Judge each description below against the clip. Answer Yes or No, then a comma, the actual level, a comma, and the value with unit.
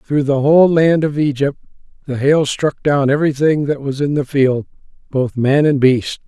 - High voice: No, medium, 140 Hz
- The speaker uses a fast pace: No, average, 190 wpm